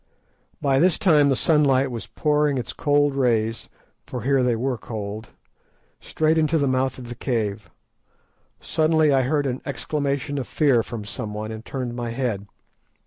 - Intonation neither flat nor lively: Yes, average, 3.8 semitones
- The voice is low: Yes, low, 130 Hz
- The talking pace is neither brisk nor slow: Yes, average, 160 wpm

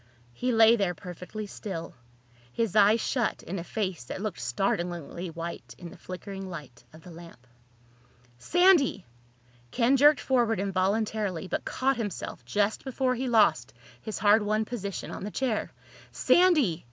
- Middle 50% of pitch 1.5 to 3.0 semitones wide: No, average, 4.7 semitones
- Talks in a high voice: Yes, high, 205 Hz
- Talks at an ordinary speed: Yes, average, 150 wpm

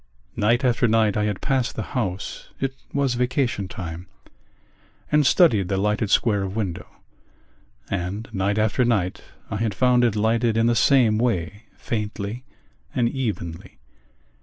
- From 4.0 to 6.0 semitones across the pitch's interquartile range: No, average, 3.4 semitones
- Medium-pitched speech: No, low, 110 Hz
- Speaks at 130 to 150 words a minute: Yes, average, 145 wpm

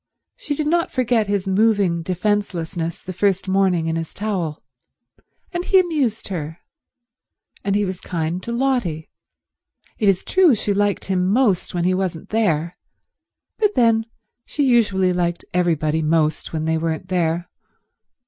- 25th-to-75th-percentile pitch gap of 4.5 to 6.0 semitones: Yes, average, 4.9 semitones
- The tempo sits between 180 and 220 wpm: No, average, 150 wpm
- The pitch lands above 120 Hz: Yes, high, 190 Hz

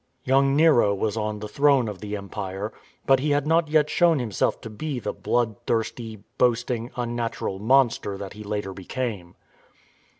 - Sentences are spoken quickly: No, average, 160 wpm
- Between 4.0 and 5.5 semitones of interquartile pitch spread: Yes, average, 4.6 semitones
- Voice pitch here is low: Yes, low, 115 Hz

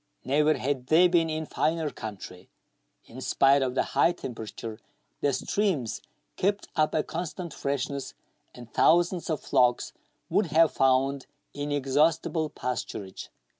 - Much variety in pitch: No, average, 4.1 semitones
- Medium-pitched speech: Yes, medium, 145 Hz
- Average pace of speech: No, slow, 130 wpm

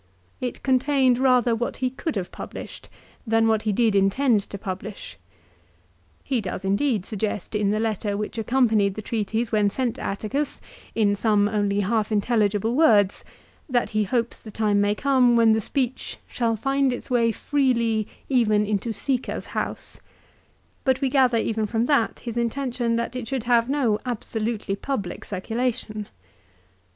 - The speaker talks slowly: No, average, 165 wpm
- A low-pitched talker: No, high, 225 Hz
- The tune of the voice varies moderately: Yes, average, 3.1 semitones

